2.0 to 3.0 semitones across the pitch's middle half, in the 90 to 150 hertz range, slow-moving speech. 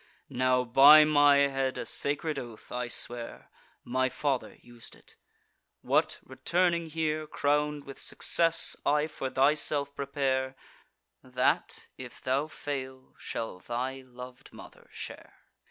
Yes: narrow, 2.5 semitones; low, 135 Hz; slow, 120 wpm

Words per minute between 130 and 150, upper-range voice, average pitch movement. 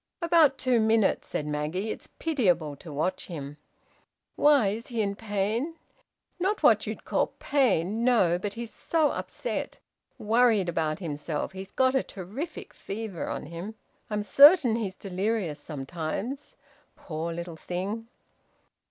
No: slow, 135 wpm; high, 205 Hz; wide, 6.1 semitones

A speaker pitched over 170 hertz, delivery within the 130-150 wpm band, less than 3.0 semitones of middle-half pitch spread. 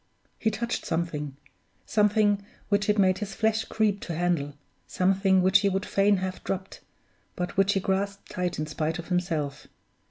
No: high, 190 Hz; average, 165 wpm; narrow, 2.6 semitones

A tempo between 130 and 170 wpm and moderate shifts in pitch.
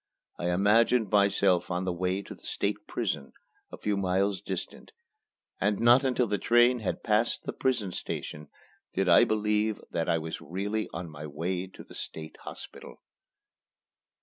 Yes: average, 160 wpm; average, 3.5 semitones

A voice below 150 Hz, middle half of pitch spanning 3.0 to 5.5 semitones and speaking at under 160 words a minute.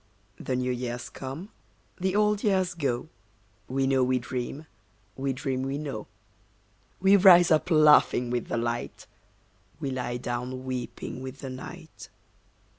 Yes: low, 135 Hz; average, 4.2 semitones; average, 140 wpm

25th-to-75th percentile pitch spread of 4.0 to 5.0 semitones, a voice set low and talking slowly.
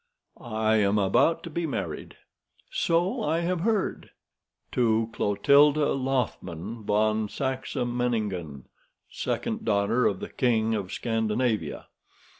Yes: average, 4.7 semitones; low, 115 Hz; slow, 110 wpm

